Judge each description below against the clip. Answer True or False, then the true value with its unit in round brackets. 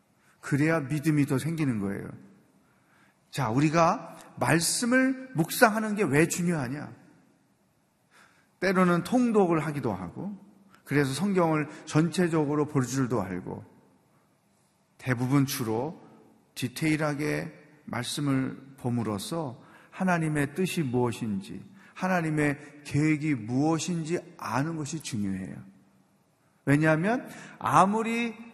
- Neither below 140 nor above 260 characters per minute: True (230 characters per minute)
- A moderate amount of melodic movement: True (4.7 semitones)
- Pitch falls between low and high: True (155 Hz)